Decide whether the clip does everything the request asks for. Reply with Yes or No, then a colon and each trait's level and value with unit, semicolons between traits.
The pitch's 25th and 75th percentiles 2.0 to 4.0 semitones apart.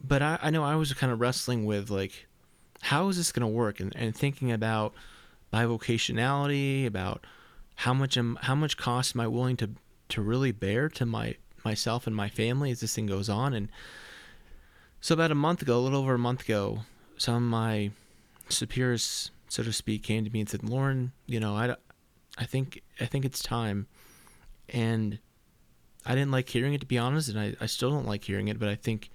Yes: average, 3.4 semitones